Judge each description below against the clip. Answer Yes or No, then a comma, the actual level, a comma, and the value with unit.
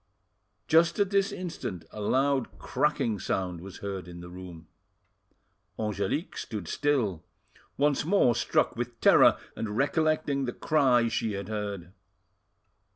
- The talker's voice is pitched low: Yes, low, 115 Hz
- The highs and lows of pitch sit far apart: Yes, wide, 7.0 semitones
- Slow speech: Yes, slow, 130 wpm